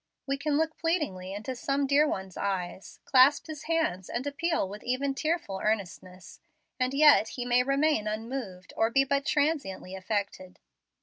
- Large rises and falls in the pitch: Yes, wide, 6.6 semitones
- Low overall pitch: No, very high, 255 Hz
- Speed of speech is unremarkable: Yes, average, 160 wpm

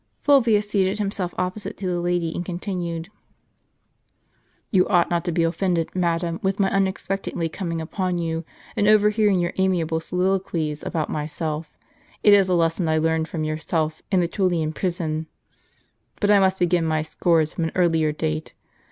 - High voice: No, medium, 175 Hz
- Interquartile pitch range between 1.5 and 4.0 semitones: Yes, average, 2.8 semitones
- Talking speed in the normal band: Yes, average, 170 wpm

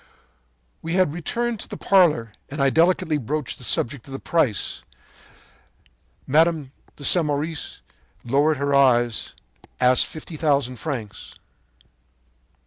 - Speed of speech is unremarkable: No, slow, 115 wpm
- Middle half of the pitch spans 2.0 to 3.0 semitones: No, average, 4.4 semitones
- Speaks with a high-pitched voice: No, medium, 140 Hz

